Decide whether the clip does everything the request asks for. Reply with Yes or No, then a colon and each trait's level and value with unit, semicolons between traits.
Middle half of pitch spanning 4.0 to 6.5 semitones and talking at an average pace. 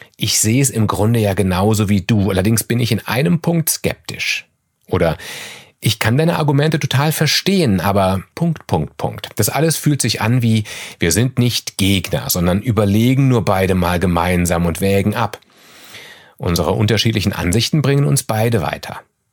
Yes: wide, 5.4 semitones; average, 165 wpm